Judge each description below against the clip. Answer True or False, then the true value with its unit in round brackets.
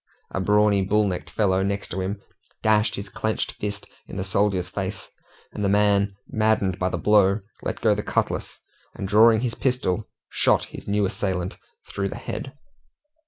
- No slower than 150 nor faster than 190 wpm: True (165 wpm)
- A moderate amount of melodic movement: False (1.8 semitones)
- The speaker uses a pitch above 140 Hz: False (100 Hz)